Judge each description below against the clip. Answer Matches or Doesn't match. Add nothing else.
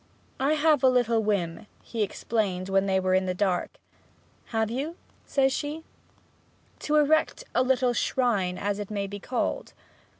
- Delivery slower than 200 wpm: Matches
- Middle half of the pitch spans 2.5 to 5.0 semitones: Doesn't match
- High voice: Matches